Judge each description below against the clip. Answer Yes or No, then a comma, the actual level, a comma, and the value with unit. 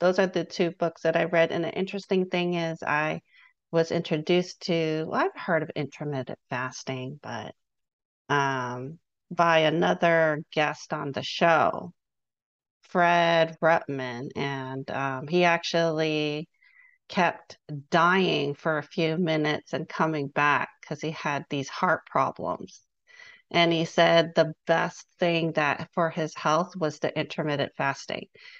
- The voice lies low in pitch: No, medium, 160 Hz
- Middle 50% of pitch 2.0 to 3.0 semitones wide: Yes, average, 2.7 semitones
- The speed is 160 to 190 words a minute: No, slow, 135 wpm